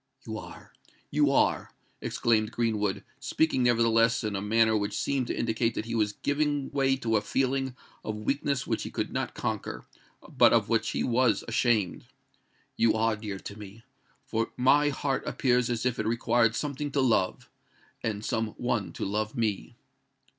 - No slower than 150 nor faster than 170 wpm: Yes, average, 165 wpm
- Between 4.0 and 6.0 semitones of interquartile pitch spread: No, average, 3.5 semitones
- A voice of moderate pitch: No, low, 115 Hz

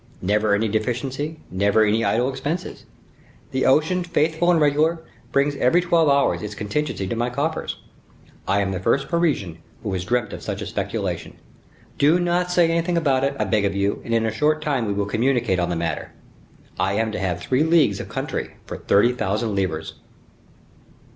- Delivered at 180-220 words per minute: Yes, average, 185 wpm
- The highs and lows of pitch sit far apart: Yes, wide, 7.2 semitones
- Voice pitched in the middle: No, low, 125 Hz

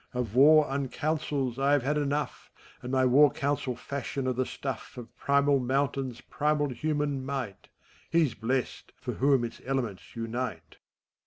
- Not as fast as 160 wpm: Yes, average, 150 wpm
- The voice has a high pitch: No, low, 135 Hz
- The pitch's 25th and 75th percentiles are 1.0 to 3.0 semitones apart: Yes, narrow, 2.5 semitones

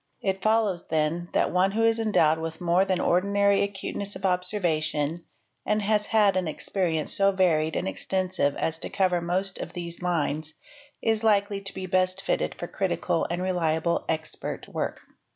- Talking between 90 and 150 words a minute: No, average, 170 wpm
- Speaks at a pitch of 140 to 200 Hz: Yes, medium, 185 Hz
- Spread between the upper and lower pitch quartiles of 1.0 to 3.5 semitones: Yes, average, 3.2 semitones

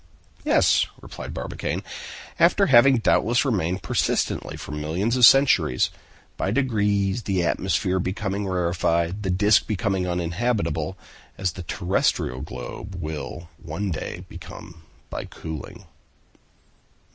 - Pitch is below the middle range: Yes, very low, 95 Hz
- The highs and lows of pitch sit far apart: No, average, 3.7 semitones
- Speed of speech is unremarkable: No, slow, 110 wpm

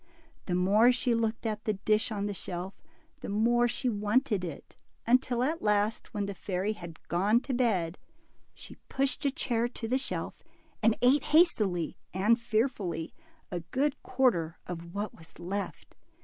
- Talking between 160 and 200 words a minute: Yes, average, 165 wpm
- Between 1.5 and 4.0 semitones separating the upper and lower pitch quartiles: No, average, 4.6 semitones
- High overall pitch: Yes, high, 215 Hz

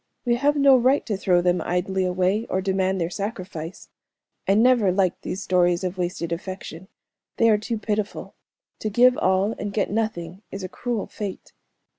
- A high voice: Yes, high, 195 Hz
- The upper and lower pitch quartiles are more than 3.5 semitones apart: No, average, 3.2 semitones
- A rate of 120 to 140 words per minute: No, average, 175 wpm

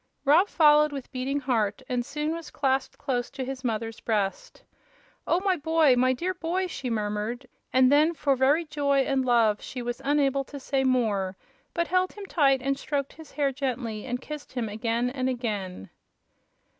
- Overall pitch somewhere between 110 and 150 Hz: No, very high, 265 Hz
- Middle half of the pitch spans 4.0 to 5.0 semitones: No, average, 3.6 semitones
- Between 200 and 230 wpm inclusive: No, average, 180 wpm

